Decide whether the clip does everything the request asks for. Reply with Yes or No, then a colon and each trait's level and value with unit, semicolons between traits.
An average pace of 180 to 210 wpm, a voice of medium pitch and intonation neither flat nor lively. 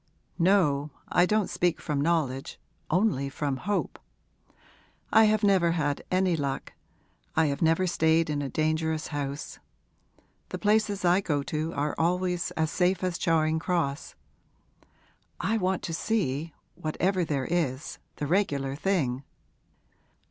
No: slow, 135 wpm; medium, 165 Hz; average, 4.1 semitones